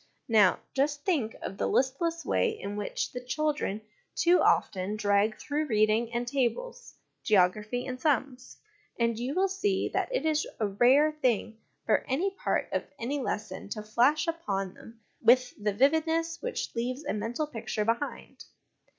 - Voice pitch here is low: No, very high, 250 Hz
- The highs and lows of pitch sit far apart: Yes, wide, 6.1 semitones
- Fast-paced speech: No, average, 160 wpm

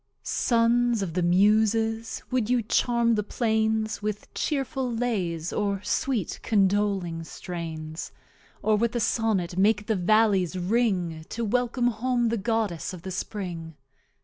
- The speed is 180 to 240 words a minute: No, slow, 135 wpm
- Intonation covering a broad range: No, average, 4.0 semitones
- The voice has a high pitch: Yes, high, 215 Hz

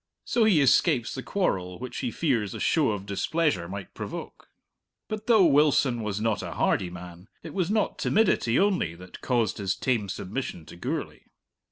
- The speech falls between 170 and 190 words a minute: Yes, average, 175 wpm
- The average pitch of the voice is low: Yes, low, 120 Hz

